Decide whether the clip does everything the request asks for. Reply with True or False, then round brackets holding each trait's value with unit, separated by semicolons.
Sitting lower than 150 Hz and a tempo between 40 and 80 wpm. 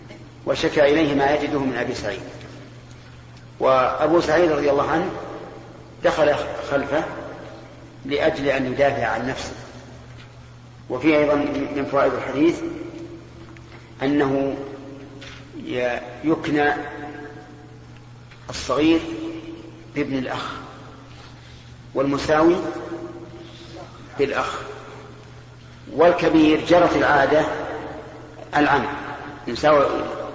True (140 Hz; 70 wpm)